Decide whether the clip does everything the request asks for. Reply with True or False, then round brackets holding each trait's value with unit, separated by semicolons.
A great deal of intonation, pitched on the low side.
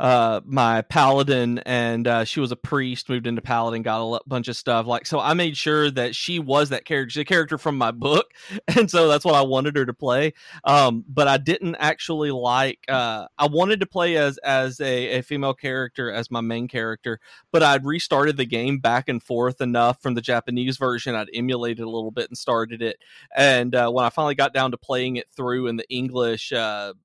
False (3.4 semitones; 125 Hz)